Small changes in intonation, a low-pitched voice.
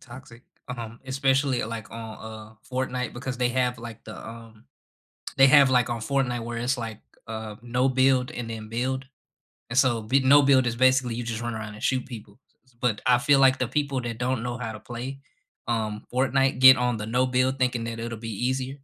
Yes: narrow, 2.3 semitones; low, 125 Hz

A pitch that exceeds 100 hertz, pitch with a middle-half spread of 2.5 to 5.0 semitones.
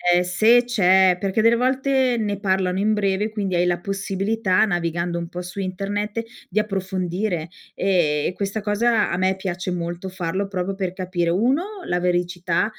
Yes: high, 190 Hz; average, 2.8 semitones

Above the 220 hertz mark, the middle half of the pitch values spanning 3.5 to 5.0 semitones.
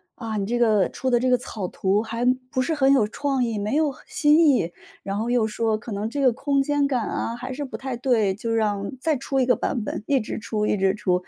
Yes: high, 240 Hz; average, 4.0 semitones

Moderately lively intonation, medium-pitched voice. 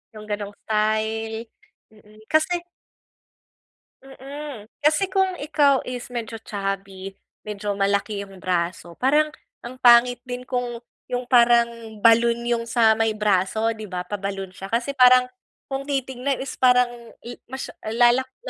No: average, 3.7 semitones; high, 235 Hz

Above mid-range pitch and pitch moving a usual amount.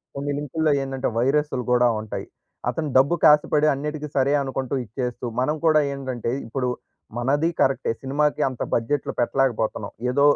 No: low, 135 Hz; average, 3.1 semitones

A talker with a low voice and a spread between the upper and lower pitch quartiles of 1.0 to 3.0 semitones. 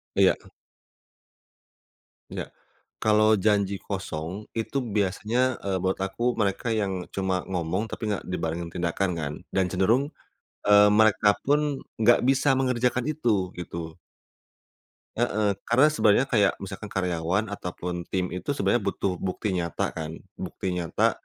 No: low, 100 Hz; average, 3.7 semitones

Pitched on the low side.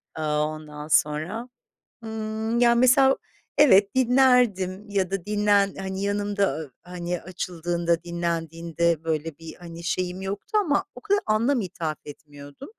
No: medium, 185 Hz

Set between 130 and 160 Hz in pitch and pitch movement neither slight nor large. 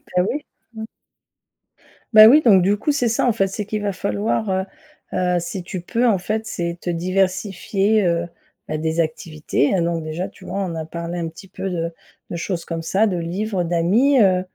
No: medium, 185 Hz; average, 3.6 semitones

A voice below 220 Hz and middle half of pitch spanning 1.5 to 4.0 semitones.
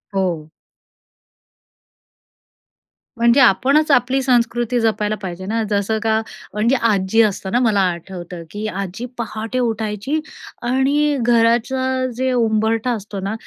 No: high, 225 Hz; average, 3.5 semitones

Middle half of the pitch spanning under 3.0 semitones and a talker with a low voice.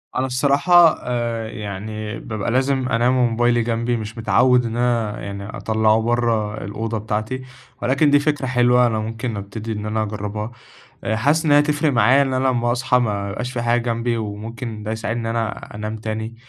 Yes: narrow, 2.5 semitones; low, 115 Hz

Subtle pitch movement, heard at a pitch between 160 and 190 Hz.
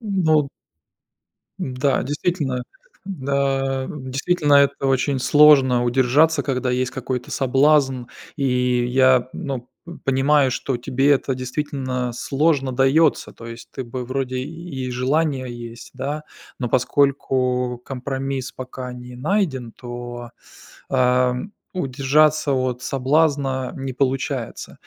No: narrow, 2.1 semitones; low, 130 Hz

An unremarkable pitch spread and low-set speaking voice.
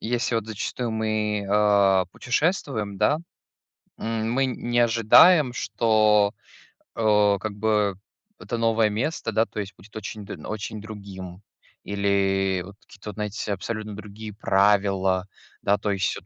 No: narrow, 2.1 semitones; low, 105 Hz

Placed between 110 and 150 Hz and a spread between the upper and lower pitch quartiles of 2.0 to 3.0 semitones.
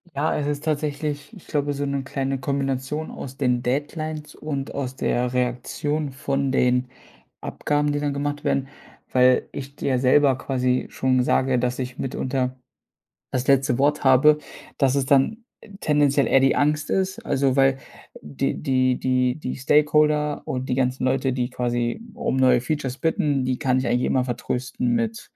Yes: low, 135 Hz; narrow, 2.4 semitones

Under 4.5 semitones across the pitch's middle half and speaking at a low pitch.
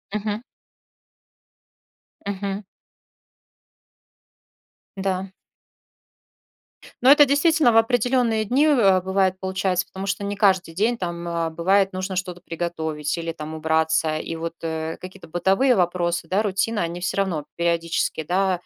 No: average, 3.2 semitones; medium, 185 Hz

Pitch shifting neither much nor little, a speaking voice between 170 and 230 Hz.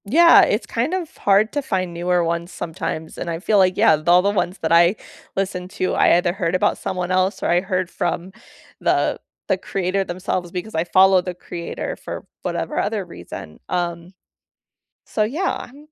No: narrow, 2.3 semitones; medium, 185 Hz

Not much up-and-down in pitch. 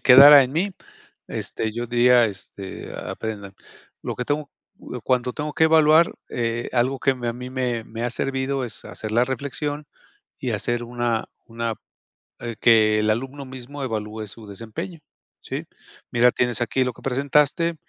No: average, 3.1 semitones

